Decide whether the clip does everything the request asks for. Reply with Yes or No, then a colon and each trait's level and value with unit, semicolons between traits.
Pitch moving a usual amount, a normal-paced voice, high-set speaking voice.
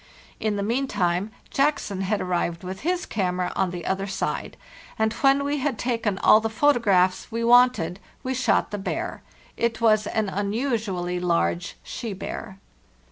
Yes: average, 4.3 semitones; average, 165 wpm; high, 210 Hz